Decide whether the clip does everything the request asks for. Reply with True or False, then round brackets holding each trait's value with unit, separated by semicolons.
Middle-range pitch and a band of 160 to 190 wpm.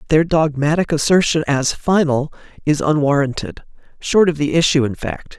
False (150 Hz; 145 wpm)